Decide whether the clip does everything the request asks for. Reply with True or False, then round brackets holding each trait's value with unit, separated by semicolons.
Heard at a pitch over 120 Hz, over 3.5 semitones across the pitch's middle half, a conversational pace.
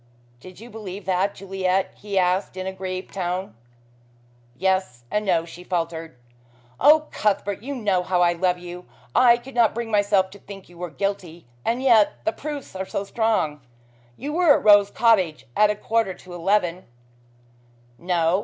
False (190 Hz; 3.0 semitones; 175 wpm)